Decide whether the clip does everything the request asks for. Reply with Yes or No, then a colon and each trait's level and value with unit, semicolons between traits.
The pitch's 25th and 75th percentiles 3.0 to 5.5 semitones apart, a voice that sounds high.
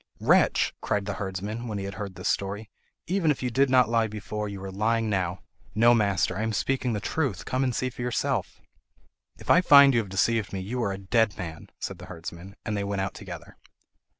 No: average, 3.8 semitones; low, 105 Hz